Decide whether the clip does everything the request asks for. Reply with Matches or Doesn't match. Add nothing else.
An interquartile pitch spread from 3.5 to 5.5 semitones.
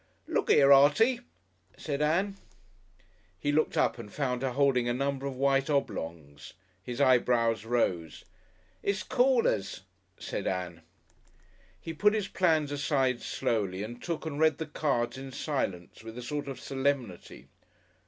Matches